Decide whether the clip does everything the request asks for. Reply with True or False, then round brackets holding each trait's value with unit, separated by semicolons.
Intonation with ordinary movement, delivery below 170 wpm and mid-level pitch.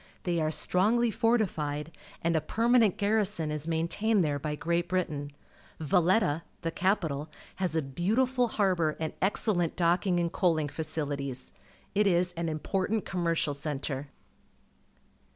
True (4.2 semitones; 140 wpm; 170 Hz)